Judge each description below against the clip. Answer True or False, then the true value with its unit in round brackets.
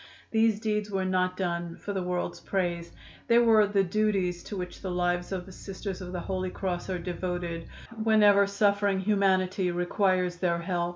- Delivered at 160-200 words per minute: True (175 wpm)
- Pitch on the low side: False (185 Hz)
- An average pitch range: False (2.2 semitones)